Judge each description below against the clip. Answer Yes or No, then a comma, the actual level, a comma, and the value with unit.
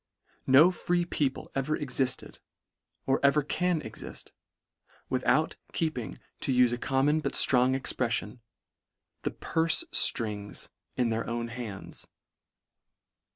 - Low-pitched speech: Yes, low, 130 Hz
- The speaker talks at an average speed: No, slow, 115 wpm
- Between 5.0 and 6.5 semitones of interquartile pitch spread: No, average, 4.1 semitones